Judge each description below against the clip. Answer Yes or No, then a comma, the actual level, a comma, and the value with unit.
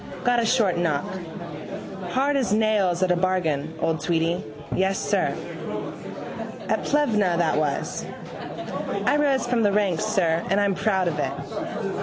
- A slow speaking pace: No, average, 145 wpm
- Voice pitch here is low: No, high, 190 Hz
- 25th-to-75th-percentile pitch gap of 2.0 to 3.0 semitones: No, average, 4.6 semitones